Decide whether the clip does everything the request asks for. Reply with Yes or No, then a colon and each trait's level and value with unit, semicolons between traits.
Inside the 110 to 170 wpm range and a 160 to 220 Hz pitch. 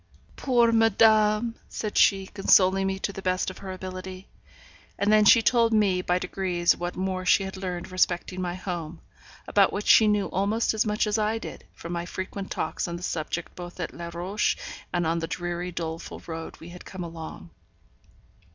No: average, 190 wpm; medium, 185 Hz